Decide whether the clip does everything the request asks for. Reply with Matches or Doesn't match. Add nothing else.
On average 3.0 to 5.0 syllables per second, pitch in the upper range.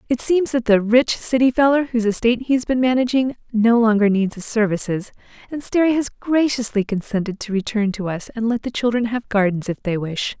Doesn't match